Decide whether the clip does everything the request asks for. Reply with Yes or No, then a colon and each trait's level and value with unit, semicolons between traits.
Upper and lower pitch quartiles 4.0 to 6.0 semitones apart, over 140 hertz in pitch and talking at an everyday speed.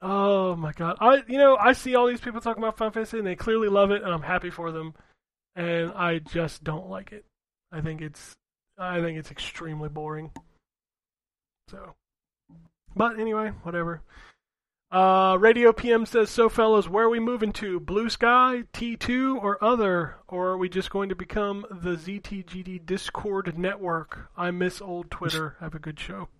Yes: average, 4.7 semitones; medium, 185 Hz; average, 185 wpm